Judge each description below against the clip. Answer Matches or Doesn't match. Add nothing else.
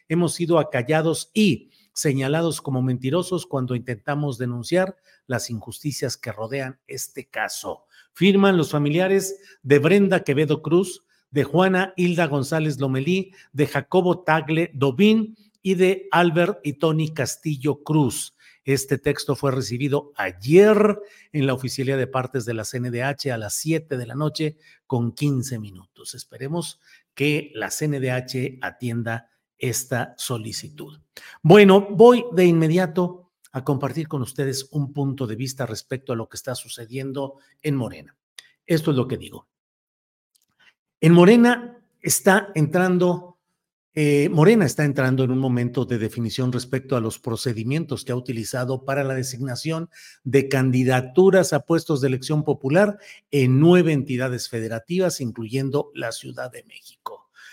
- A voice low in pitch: Doesn't match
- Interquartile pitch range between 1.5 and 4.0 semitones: Doesn't match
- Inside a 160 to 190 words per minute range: Doesn't match